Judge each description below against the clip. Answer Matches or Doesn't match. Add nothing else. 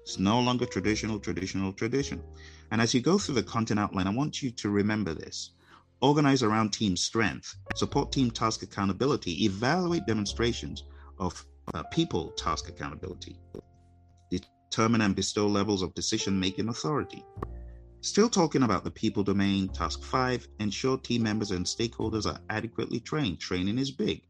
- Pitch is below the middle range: Matches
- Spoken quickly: Doesn't match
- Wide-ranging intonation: Doesn't match